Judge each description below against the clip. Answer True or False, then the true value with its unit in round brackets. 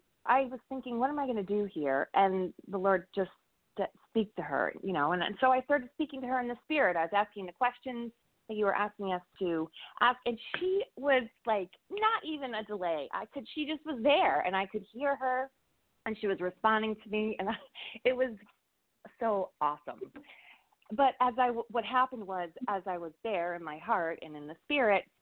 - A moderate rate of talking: False (215 wpm)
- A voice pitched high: True (220 Hz)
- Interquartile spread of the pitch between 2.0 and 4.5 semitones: False (5.3 semitones)